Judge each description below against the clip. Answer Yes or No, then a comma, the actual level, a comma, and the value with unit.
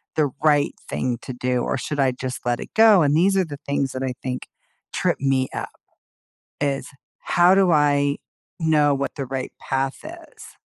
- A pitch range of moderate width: Yes, average, 3.2 semitones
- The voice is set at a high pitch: No, medium, 140 Hz